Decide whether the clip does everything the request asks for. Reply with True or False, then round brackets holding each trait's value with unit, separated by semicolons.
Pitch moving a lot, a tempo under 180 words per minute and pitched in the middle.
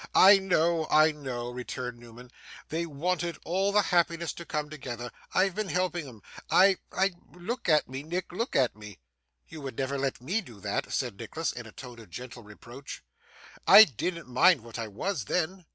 False (6.6 semitones; 185 wpm; 150 Hz)